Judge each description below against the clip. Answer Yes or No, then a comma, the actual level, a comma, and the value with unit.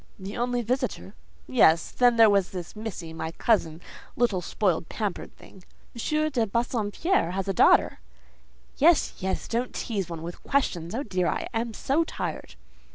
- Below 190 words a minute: Yes, average, 155 wpm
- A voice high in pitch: Yes, high, 215 Hz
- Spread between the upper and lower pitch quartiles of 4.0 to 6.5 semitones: Yes, average, 5.1 semitones